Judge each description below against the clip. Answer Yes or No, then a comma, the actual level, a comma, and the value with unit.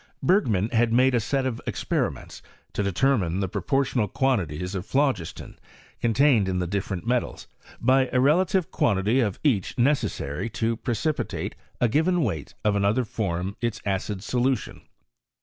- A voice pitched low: Yes, low, 115 Hz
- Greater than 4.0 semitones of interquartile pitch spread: Yes, average, 5.2 semitones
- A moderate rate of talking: Yes, average, 150 wpm